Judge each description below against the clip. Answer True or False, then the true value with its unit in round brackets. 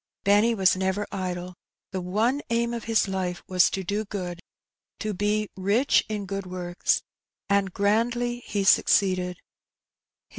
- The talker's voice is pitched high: True (200 Hz)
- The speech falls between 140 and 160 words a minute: True (150 wpm)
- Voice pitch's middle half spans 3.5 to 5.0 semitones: False (2.7 semitones)